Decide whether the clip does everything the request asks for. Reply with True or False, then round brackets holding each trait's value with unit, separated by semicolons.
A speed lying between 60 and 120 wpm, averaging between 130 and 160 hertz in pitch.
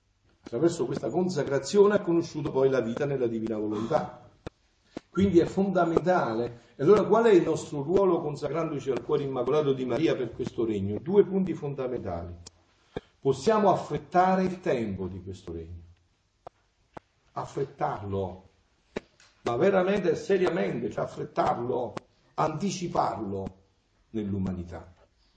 True (115 wpm; 135 Hz)